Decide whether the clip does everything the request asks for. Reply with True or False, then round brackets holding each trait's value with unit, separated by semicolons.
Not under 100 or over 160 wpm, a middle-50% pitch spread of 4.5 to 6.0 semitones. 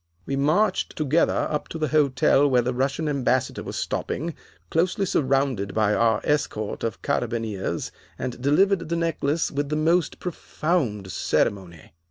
True (145 wpm; 5.3 semitones)